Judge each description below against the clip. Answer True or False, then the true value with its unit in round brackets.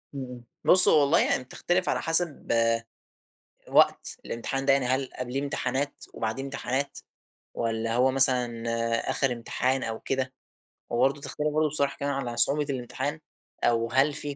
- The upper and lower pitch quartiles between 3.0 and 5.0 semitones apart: False (2.5 semitones)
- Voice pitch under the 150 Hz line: True (135 Hz)